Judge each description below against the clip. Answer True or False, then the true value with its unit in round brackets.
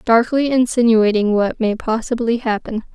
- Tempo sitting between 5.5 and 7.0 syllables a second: False (4.7 syllables/s)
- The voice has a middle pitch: False (230 Hz)